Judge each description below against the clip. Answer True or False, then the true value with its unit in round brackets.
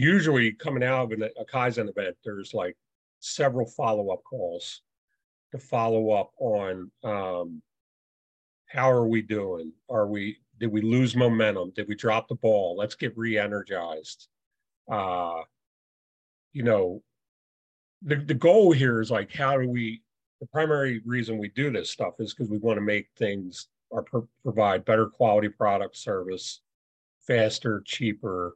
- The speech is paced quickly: False (150 wpm)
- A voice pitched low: True (115 Hz)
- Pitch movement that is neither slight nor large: True (3.6 semitones)